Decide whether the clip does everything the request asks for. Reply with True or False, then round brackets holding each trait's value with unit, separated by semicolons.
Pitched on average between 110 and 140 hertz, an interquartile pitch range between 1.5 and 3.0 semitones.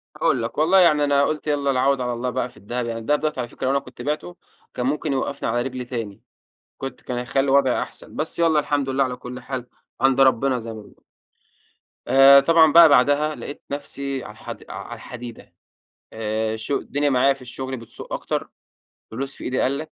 True (135 Hz; 2.6 semitones)